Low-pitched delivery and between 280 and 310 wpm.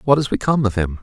Yes: low, 115 Hz; fast, 295 wpm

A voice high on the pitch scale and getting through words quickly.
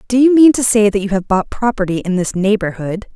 Yes: high, 210 Hz; fast, 245 wpm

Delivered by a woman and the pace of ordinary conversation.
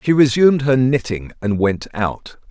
No: male; average, 170 wpm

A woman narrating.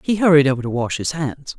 Yes: female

